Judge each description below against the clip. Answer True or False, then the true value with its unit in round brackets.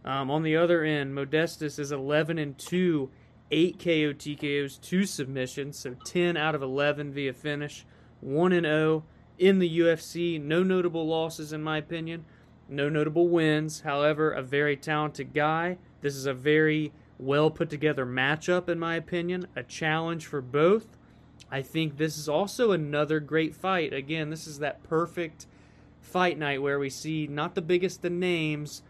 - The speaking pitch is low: False (155 Hz)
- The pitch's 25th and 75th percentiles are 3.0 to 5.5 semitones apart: False (2.5 semitones)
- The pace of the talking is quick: False (165 wpm)